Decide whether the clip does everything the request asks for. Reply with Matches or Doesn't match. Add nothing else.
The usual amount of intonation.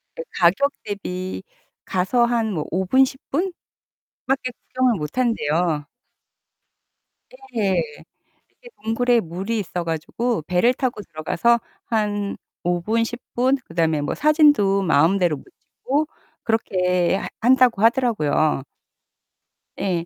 Doesn't match